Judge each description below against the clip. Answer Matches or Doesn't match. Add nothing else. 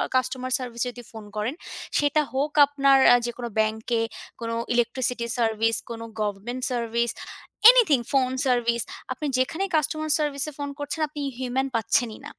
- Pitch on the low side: Doesn't match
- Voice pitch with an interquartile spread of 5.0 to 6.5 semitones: Doesn't match